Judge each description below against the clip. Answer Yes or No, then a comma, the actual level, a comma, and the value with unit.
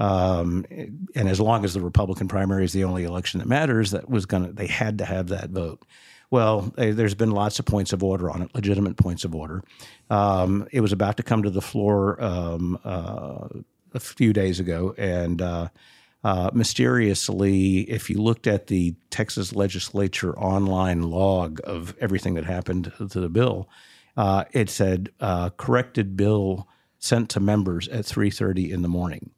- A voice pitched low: Yes, very low, 95 Hz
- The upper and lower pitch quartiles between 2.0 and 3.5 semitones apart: Yes, narrow, 2.5 semitones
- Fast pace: No, average, 175 wpm